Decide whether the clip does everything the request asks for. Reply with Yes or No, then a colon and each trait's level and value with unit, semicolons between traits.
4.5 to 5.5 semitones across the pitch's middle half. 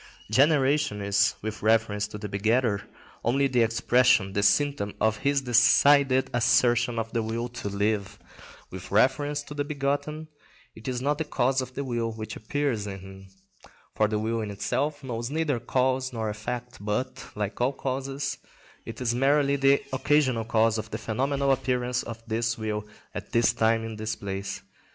No: average, 3.8 semitones